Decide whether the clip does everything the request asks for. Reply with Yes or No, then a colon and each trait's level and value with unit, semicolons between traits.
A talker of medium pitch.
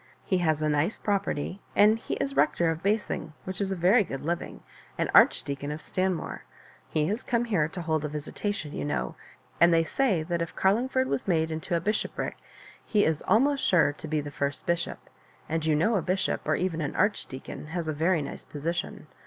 Yes: medium, 170 Hz